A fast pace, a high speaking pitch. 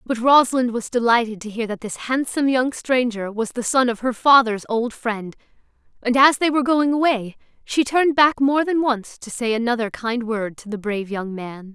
Yes: fast, 210 wpm; high, 240 Hz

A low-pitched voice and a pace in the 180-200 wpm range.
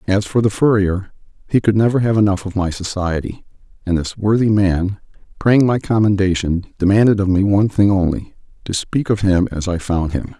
Yes: low, 100 Hz; average, 185 wpm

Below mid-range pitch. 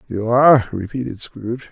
Yes: low, 120 Hz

